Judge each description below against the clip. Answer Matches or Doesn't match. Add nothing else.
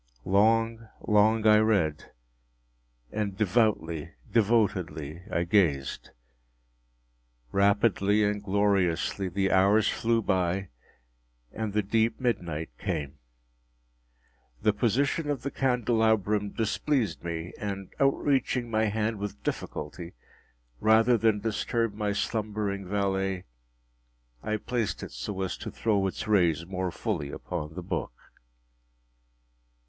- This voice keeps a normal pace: Doesn't match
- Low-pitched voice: Matches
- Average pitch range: Matches